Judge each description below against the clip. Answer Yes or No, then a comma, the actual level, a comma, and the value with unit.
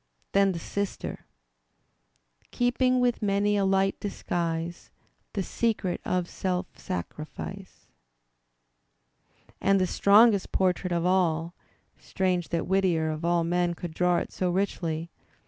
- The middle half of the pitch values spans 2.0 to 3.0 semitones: Yes, narrow, 2.6 semitones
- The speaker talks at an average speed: No, slow, 120 wpm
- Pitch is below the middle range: No, medium, 185 Hz